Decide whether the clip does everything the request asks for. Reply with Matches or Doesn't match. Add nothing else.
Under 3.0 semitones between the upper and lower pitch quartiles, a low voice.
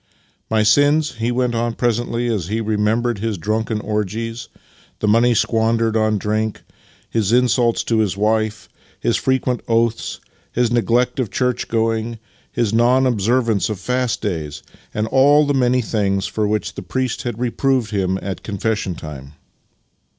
Matches